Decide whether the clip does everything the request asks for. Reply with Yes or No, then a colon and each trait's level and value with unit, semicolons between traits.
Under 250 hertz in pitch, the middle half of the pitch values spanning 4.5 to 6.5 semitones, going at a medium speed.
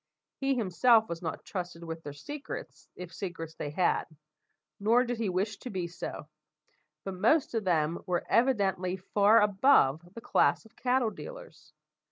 Yes: high, 190 Hz; average, 5.2 semitones; average, 160 wpm